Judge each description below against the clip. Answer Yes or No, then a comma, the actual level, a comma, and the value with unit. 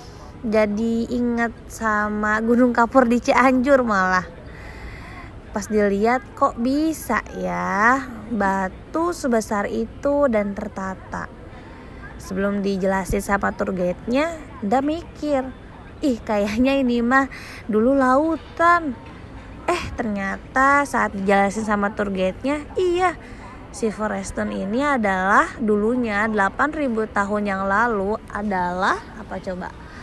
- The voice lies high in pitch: Yes, high, 220 Hz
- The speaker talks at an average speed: Yes, average, 100 wpm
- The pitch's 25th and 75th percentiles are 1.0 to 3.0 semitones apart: No, average, 4.8 semitones